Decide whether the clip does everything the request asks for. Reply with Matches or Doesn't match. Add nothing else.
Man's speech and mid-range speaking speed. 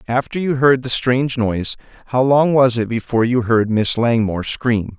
Matches